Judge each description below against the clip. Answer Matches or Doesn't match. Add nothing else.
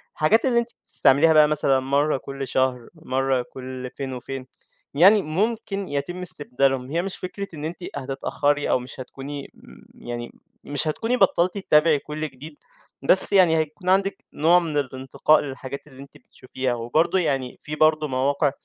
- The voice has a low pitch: Doesn't match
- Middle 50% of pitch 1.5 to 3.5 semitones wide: Doesn't match